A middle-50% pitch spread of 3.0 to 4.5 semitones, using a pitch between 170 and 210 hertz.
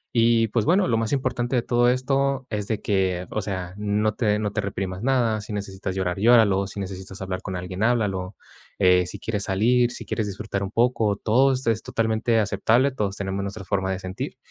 No: average, 3.5 semitones; low, 105 Hz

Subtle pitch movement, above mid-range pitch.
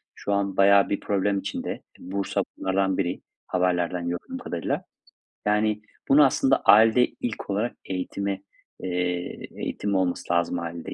No: narrow, 2.3 semitones; very low, 95 Hz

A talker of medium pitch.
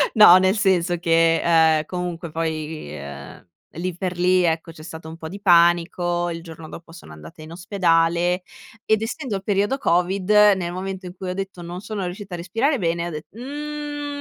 Yes: medium, 175 Hz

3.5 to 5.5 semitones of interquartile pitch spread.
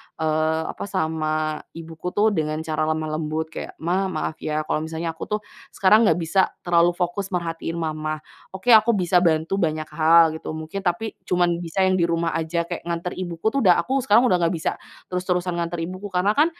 No: average, 2.8 semitones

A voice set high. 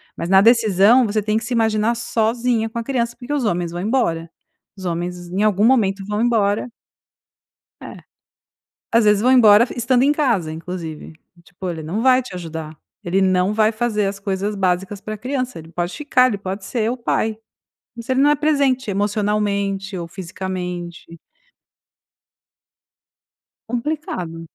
Yes: high, 210 Hz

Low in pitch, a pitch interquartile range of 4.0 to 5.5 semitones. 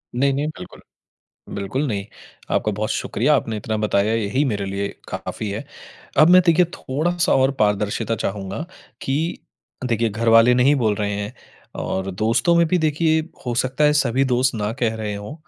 Yes: low, 115 Hz; average, 5.1 semitones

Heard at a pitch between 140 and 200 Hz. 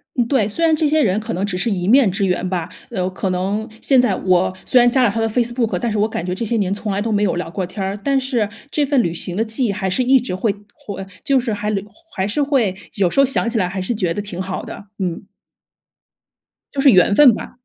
No: high, 210 Hz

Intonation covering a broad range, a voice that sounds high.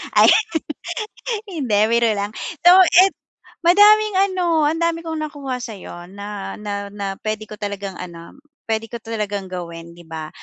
Yes: wide, 8.4 semitones; high, 215 Hz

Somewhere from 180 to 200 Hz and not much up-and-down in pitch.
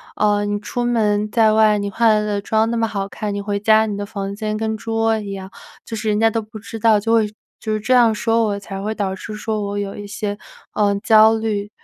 No: high, 215 Hz; narrow, 1.4 semitones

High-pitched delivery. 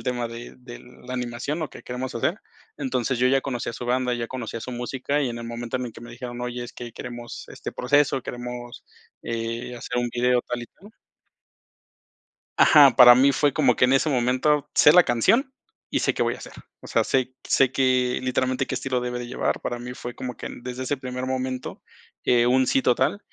No: low, 125 Hz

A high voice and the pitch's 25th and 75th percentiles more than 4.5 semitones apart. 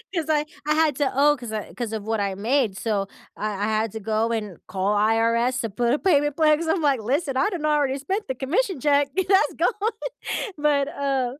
Yes: very high, 265 Hz; average, 5.2 semitones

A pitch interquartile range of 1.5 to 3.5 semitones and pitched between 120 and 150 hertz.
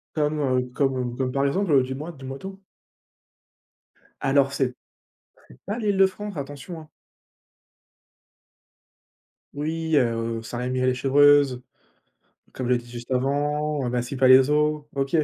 Yes: average, 2.9 semitones; low, 135 Hz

